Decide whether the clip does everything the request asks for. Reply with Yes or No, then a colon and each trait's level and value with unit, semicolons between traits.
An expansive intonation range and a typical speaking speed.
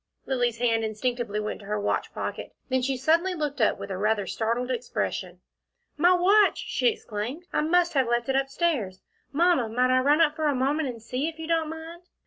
No: wide, 5.7 semitones; fast, 210 wpm